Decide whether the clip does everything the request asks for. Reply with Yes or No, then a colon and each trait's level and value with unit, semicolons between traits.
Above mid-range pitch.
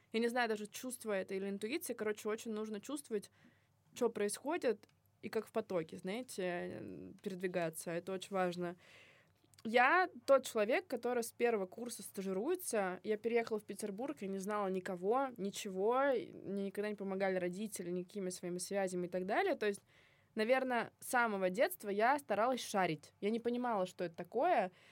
Yes: high, 210 Hz